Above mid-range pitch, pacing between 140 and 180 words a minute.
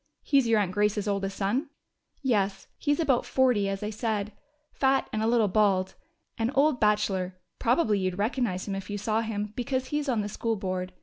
No: high, 210 Hz; average, 195 wpm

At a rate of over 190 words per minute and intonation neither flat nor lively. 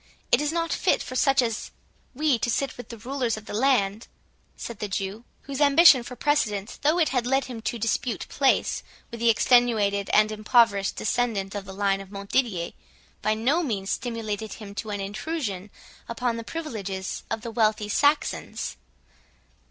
No: average, 175 wpm; average, 4.3 semitones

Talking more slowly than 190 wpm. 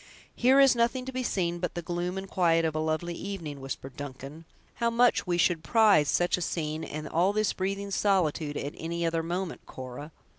No: average, 200 wpm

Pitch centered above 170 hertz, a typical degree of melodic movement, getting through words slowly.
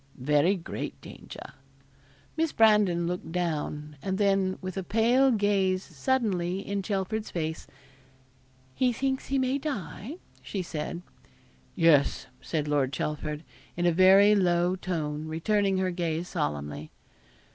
Yes: medium, 185 Hz; average, 4.4 semitones; slow, 125 wpm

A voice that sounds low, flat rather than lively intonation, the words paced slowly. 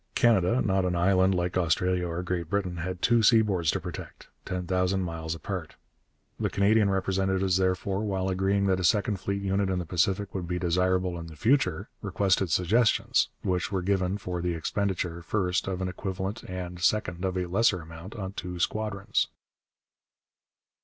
No: very low, 95 Hz; narrow, 1.8 semitones; average, 170 wpm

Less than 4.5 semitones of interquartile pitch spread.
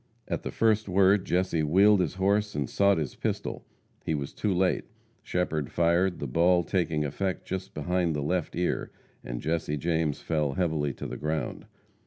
Yes: average, 3.7 semitones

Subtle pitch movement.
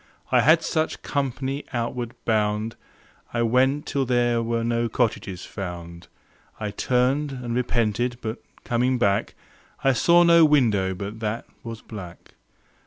No: average, 3.4 semitones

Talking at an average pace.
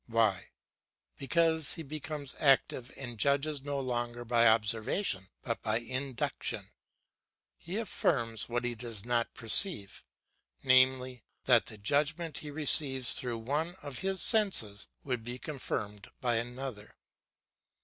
No: slow, 125 wpm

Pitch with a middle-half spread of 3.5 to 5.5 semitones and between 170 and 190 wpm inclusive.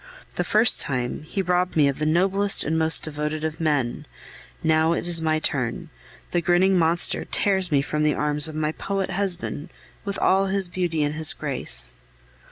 No: average, 3.1 semitones; average, 180 wpm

